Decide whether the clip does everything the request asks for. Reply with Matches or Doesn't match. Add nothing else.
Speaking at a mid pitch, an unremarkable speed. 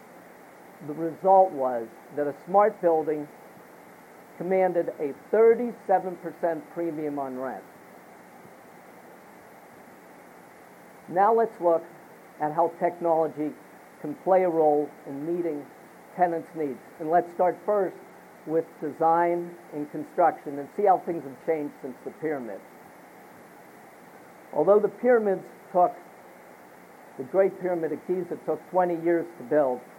Doesn't match